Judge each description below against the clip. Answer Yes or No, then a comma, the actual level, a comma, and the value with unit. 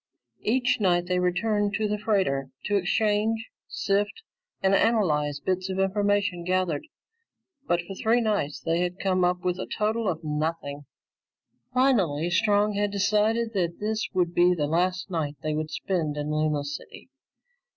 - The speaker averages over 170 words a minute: No, average, 160 wpm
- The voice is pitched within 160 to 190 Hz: Yes, medium, 185 Hz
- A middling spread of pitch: Yes, average, 4.1 semitones